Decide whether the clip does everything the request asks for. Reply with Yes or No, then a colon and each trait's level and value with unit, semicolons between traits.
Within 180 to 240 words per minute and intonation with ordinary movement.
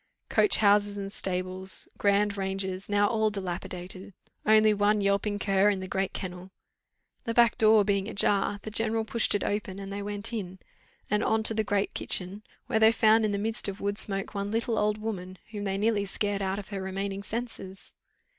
No: average, 195 wpm; narrow, 1.7 semitones